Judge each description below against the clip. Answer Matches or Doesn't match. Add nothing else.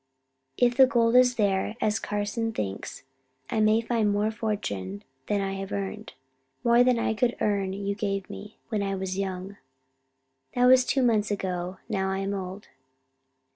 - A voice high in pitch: Matches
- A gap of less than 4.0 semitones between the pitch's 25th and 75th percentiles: Matches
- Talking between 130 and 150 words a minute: Doesn't match